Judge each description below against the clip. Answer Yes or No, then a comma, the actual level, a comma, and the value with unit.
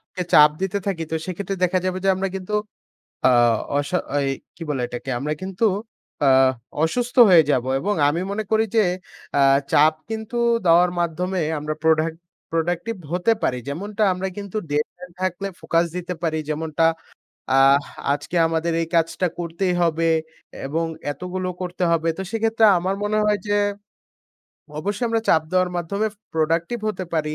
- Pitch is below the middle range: No, medium, 175 Hz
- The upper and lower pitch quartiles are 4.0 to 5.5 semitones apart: No, average, 3.3 semitones